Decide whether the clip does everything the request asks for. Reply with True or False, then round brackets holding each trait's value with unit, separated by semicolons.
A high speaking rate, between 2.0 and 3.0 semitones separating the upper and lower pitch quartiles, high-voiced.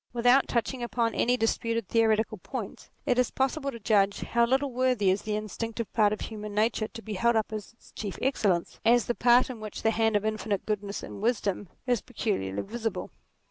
True (210 wpm; 2.4 semitones; 225 Hz)